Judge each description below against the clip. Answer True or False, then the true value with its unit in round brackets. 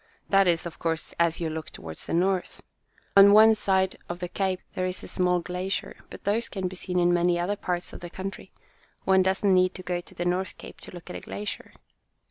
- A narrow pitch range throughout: True (1.6 semitones)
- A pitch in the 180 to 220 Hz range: True (185 Hz)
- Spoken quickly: True (230 wpm)